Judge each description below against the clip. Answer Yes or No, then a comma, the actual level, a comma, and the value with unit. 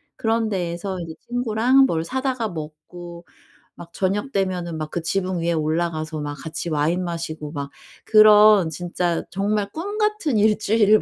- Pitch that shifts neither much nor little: Yes, average, 4.6 semitones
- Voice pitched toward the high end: No, medium, 180 Hz